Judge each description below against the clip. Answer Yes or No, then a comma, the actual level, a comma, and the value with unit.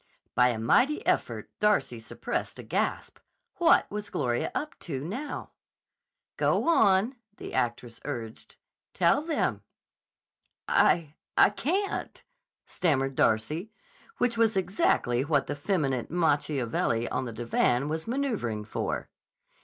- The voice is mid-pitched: Yes, medium, 150 Hz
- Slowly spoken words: Yes, slow, 120 wpm